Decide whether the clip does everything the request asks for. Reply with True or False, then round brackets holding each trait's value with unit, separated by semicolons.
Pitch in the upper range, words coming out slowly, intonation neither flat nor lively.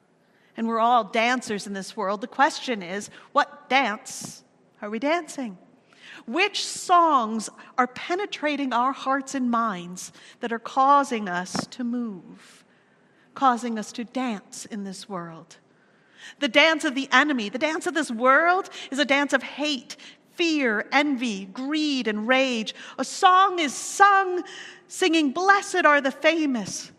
False (265 Hz; 145 wpm; 5.0 semitones)